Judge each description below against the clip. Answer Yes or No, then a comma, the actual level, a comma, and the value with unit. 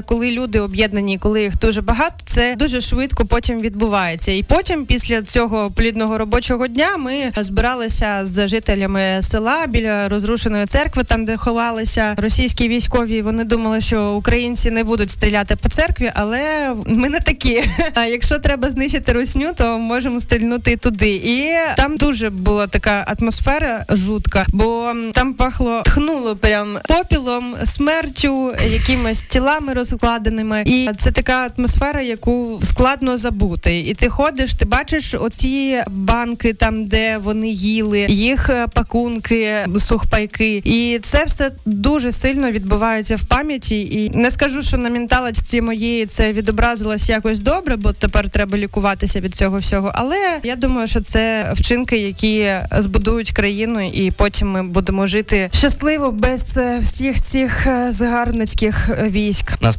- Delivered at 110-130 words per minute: No, average, 140 wpm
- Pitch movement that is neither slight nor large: Yes, average, 3.0 semitones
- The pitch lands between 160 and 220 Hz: No, high, 230 Hz